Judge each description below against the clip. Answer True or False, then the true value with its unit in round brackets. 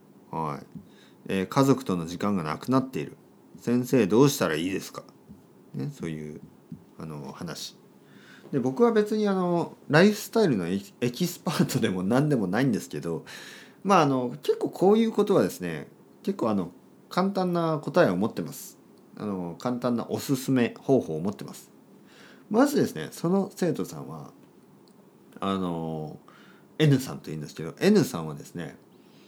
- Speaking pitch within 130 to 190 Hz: True (135 Hz)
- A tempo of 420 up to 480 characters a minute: False (310 characters per minute)